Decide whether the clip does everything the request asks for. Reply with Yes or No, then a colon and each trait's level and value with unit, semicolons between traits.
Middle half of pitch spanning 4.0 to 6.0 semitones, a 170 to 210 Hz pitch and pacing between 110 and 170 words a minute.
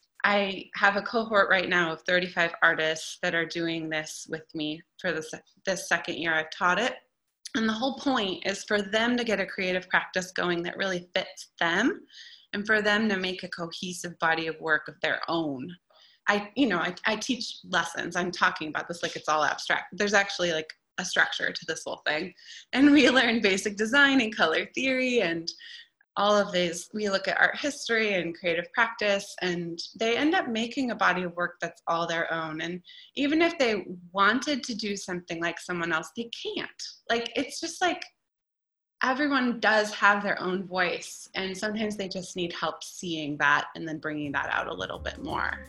No: average, 5.0 semitones; high, 190 Hz; average, 200 wpm